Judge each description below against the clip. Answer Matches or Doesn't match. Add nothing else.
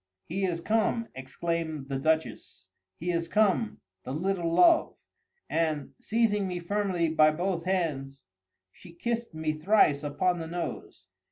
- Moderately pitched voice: Matches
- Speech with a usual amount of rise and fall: Matches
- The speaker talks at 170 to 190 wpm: Doesn't match